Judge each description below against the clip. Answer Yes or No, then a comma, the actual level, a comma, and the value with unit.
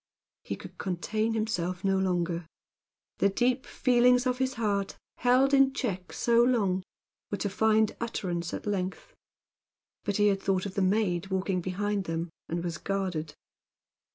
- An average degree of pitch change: Yes, average, 3.9 semitones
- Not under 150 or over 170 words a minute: Yes, average, 155 wpm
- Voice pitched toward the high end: Yes, high, 195 Hz